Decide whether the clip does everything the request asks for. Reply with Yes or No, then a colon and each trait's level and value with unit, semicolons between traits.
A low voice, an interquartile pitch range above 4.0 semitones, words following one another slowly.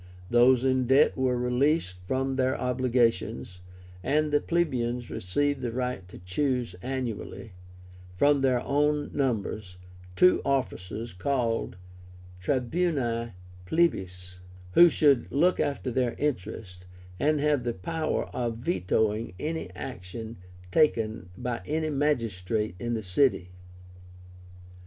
Yes: low, 125 Hz; average, 4.5 semitones; slow, 115 wpm